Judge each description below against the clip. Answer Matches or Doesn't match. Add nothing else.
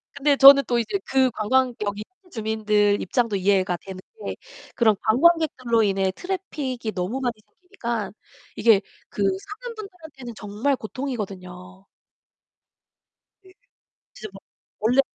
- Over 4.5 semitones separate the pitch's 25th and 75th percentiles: Matches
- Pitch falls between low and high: Doesn't match